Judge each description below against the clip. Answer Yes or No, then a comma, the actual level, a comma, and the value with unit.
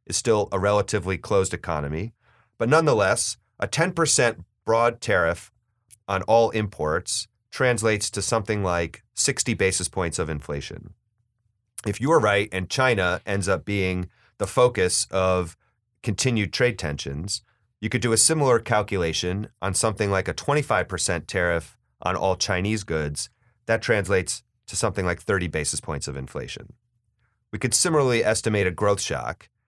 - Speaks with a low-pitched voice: Yes, low, 105 Hz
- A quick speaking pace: No, average, 145 wpm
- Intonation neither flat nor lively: Yes, average, 4.1 semitones